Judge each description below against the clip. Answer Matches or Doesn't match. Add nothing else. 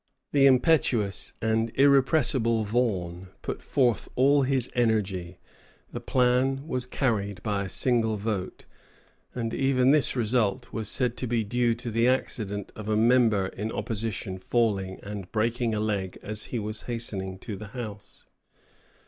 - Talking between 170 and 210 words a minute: Doesn't match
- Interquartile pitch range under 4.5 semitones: Matches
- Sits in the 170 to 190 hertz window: Doesn't match